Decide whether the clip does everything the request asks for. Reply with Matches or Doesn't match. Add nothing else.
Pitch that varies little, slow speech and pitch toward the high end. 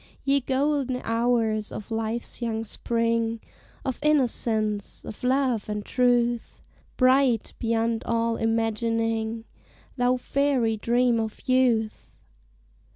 Matches